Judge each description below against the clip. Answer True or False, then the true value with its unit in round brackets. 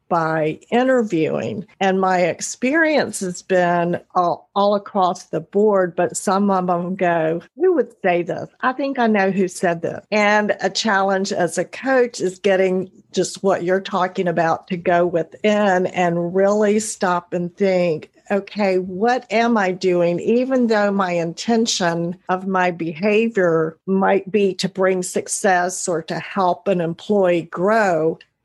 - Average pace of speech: True (150 wpm)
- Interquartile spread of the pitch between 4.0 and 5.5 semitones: False (2.9 semitones)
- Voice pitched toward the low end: False (185 Hz)